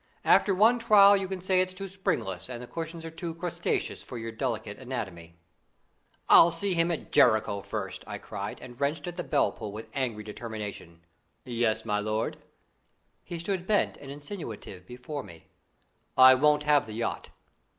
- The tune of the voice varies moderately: No, wide, 8.0 semitones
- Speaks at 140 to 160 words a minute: No, average, 170 wpm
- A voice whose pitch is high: No, medium, 140 Hz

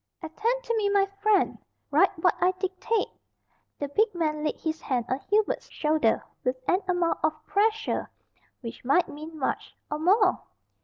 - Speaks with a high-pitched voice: Yes, very high, 350 Hz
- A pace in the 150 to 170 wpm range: Yes, average, 160 wpm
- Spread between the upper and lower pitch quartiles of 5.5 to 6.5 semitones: No, average, 5.1 semitones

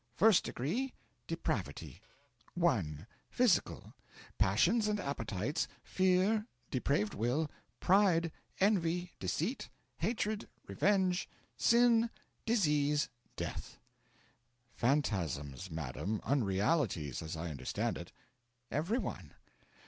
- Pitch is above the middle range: No, medium, 150 Hz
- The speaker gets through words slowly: Yes, slow, 85 wpm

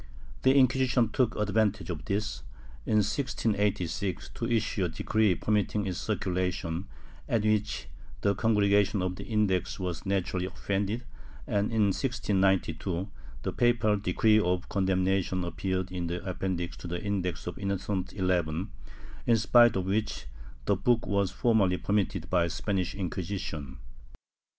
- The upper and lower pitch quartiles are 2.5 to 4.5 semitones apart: Yes, average, 2.8 semitones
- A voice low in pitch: Yes, low, 100 Hz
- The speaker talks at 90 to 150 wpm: Yes, slow, 135 wpm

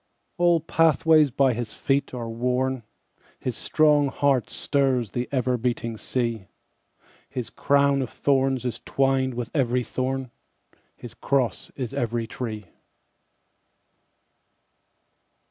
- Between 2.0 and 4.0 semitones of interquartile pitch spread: Yes, narrow, 2.5 semitones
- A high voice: No, low, 130 Hz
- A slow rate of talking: Yes, slow, 100 wpm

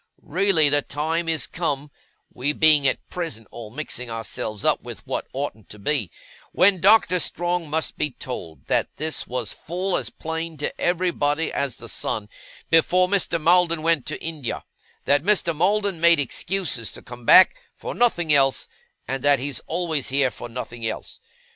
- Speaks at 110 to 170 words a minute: Yes, average, 165 wpm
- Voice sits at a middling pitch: Yes, medium, 155 Hz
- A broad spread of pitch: No, average, 4.4 semitones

